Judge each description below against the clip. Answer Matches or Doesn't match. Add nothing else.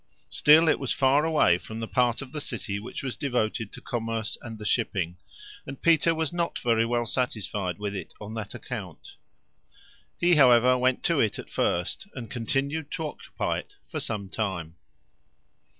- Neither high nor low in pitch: Doesn't match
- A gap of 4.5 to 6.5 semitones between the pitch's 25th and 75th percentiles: Matches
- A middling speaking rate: Matches